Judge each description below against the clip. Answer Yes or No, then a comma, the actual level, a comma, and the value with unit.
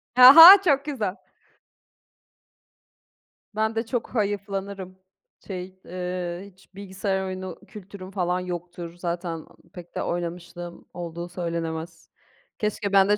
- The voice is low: No, medium, 185 Hz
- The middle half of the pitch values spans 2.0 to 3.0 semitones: Yes, narrow, 2.5 semitones